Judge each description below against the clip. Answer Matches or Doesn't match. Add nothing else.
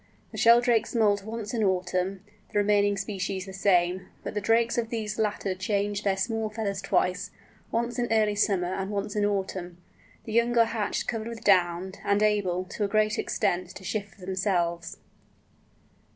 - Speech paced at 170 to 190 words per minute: Matches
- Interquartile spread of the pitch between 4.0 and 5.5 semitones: Doesn't match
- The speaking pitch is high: Matches